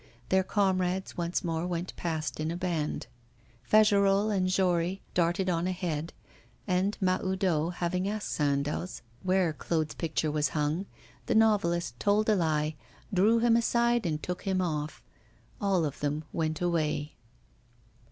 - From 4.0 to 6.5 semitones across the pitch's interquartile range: No, average, 3.4 semitones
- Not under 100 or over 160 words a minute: Yes, average, 140 wpm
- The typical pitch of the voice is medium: Yes, medium, 180 Hz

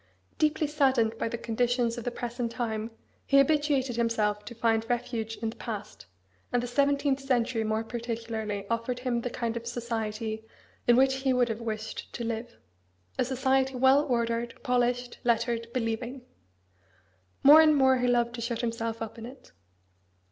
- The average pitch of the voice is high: Yes, high, 240 Hz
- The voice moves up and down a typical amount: No, narrow, 2.1 semitones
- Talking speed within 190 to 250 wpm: No, average, 170 wpm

